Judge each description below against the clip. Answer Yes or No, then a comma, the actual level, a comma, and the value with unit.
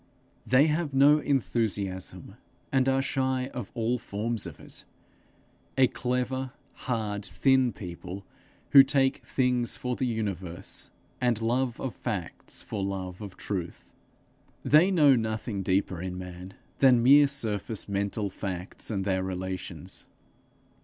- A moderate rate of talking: No, slow, 130 wpm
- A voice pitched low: Yes, low, 115 Hz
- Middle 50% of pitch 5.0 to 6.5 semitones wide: Yes, wide, 5.4 semitones